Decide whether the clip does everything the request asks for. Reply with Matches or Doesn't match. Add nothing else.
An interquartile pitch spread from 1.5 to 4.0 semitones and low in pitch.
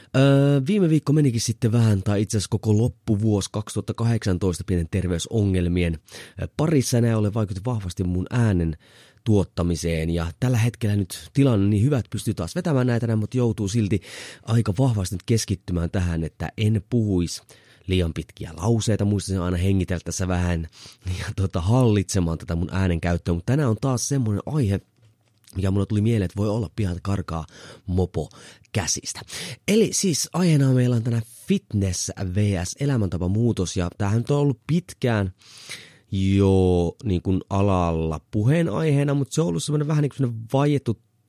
Doesn't match